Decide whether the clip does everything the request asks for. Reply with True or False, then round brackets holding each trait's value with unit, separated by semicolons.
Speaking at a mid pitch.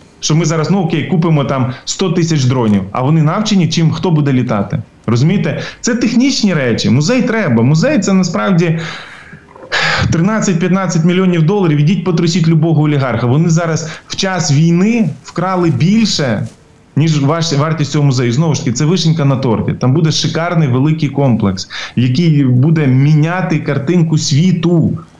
True (160 Hz)